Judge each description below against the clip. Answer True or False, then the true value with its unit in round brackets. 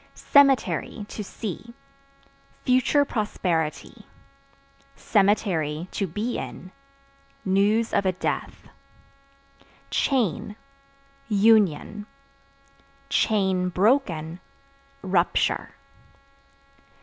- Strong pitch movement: False (4.0 semitones)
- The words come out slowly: True (55 wpm)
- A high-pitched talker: True (205 Hz)